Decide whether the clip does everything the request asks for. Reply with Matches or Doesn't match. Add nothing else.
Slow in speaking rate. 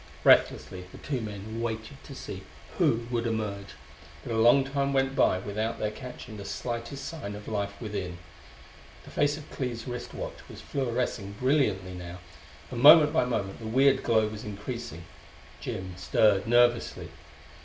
Doesn't match